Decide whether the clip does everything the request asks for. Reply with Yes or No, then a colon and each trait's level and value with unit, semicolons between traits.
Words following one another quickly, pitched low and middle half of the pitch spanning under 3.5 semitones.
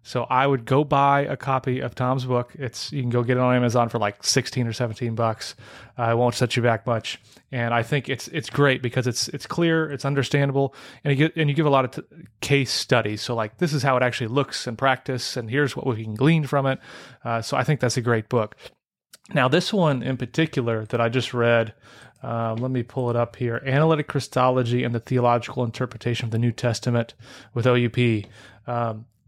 Yes: fast, 225 wpm; low, 125 Hz; narrow, 2.6 semitones